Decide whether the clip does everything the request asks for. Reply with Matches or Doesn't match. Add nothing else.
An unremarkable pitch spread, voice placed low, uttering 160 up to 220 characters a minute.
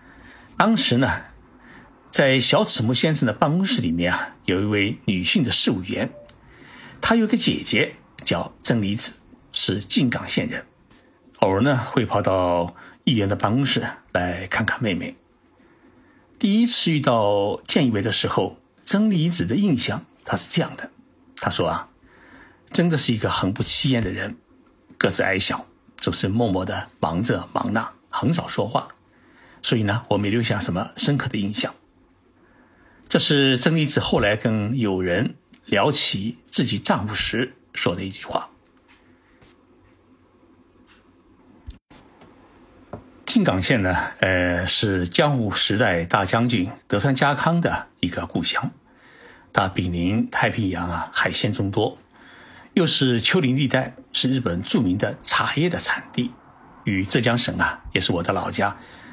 Doesn't match